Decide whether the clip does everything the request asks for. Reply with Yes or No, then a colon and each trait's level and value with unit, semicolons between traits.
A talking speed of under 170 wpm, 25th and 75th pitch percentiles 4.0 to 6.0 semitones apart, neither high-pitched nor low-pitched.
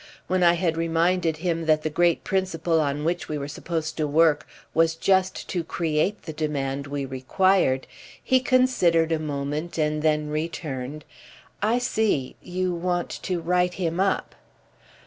No: average, 150 wpm; average, 2.9 semitones; medium, 165 Hz